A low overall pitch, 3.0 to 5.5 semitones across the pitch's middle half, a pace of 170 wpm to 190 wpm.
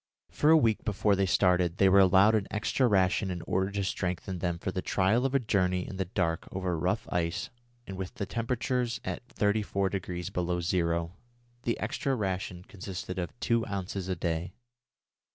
No: very low, 95 Hz; narrow, 2.6 semitones; average, 180 wpm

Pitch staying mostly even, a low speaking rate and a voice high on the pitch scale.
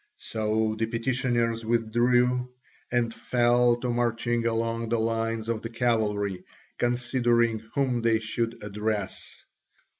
No: narrow, 1.4 semitones; slow, 115 wpm; low, 115 Hz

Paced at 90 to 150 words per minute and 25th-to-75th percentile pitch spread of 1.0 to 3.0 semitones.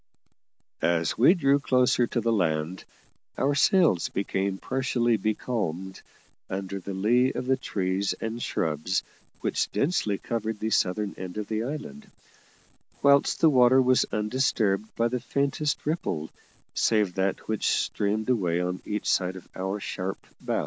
No: average, 145 wpm; average, 5.2 semitones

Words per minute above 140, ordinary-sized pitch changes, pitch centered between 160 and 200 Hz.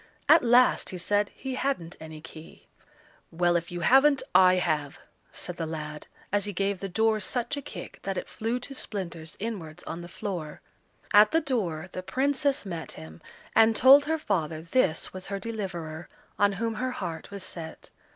No: average, 180 wpm; wide, 5.7 semitones; high, 190 Hz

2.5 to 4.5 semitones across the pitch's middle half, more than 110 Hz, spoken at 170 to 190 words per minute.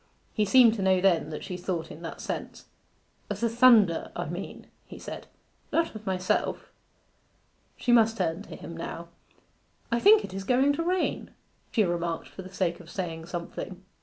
No: average, 5.1 semitones; high, 190 Hz; average, 175 wpm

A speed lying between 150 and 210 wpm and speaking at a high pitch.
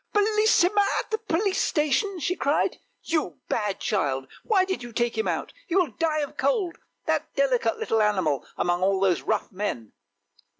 Yes: average, 175 wpm; very high, 300 Hz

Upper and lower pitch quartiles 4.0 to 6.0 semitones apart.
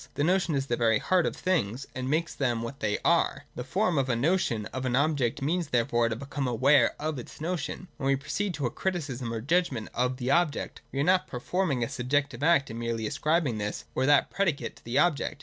Yes: average, 4.9 semitones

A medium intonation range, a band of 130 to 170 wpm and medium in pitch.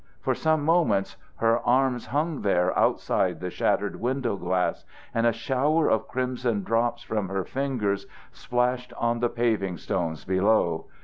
No: average, 4.6 semitones; average, 145 wpm; low, 115 Hz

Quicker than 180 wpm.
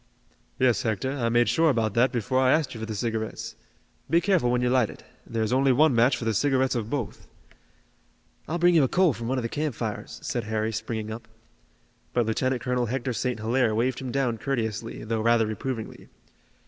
Yes: fast, 205 wpm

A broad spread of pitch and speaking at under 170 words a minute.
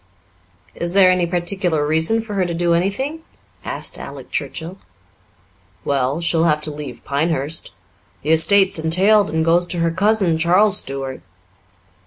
No: average, 3.3 semitones; average, 145 wpm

